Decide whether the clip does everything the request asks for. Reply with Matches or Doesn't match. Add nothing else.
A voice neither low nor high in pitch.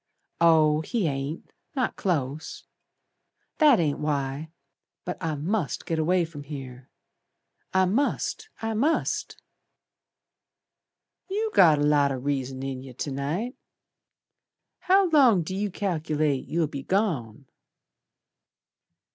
Matches